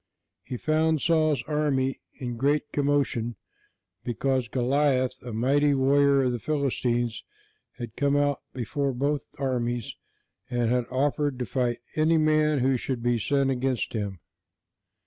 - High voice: No, low, 135 Hz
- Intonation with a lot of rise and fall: No, average, 3.0 semitones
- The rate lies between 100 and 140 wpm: Yes, slow, 135 wpm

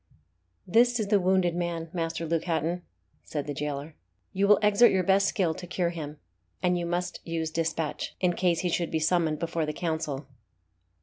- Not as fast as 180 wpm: No, average, 185 wpm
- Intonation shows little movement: Yes, narrow, 2.2 semitones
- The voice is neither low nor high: Yes, medium, 170 Hz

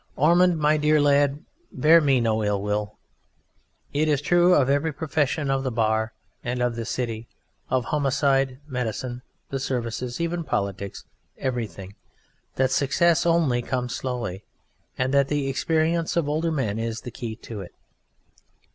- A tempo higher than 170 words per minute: No, average, 150 wpm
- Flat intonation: No, average, 4.5 semitones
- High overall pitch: No, low, 135 Hz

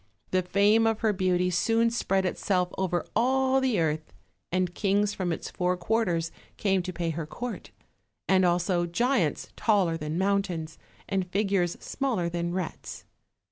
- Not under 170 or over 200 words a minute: No, average, 150 wpm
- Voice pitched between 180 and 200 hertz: Yes, medium, 185 Hz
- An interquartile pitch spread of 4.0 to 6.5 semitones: No, average, 3.2 semitones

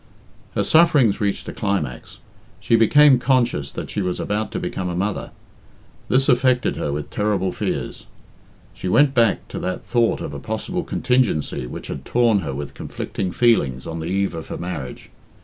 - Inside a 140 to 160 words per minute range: No, average, 175 wpm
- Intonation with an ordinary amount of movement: No, wide, 6.6 semitones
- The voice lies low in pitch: Yes, low, 100 Hz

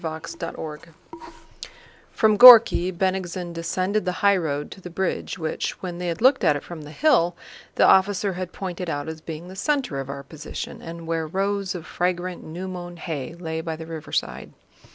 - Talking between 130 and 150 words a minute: No, average, 180 wpm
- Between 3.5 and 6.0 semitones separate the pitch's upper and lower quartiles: No, average, 2.8 semitones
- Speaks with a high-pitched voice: No, medium, 175 Hz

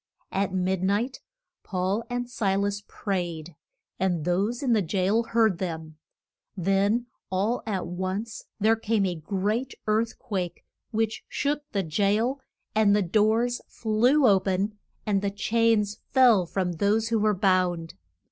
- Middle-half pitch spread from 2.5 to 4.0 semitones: Yes, average, 3.3 semitones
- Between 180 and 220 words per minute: No, average, 145 wpm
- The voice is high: Yes, high, 205 Hz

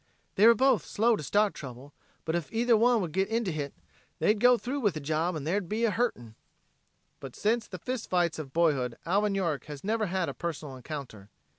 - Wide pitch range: Yes, wide, 6.7 semitones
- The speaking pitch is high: No, medium, 180 Hz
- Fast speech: Yes, fast, 210 wpm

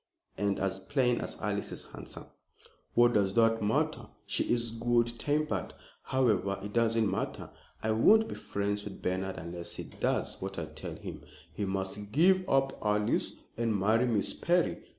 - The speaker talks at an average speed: Yes, average, 165 wpm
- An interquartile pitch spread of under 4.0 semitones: Yes, average, 3.5 semitones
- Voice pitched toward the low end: Yes, low, 110 Hz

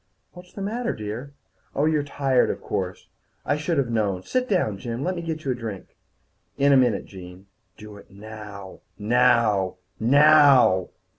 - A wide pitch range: Yes, wide, 6.3 semitones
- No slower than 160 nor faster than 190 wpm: Yes, average, 165 wpm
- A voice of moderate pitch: No, low, 125 Hz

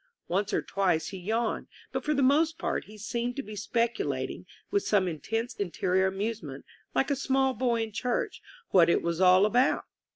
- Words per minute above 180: Yes, average, 190 wpm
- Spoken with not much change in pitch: No, average, 4.7 semitones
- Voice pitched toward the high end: Yes, high, 220 Hz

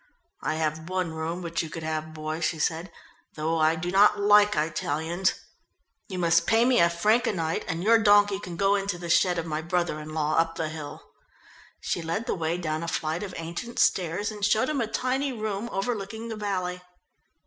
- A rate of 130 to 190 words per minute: No, fast, 205 wpm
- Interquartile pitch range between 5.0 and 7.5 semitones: No, average, 4.2 semitones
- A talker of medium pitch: Yes, medium, 175 Hz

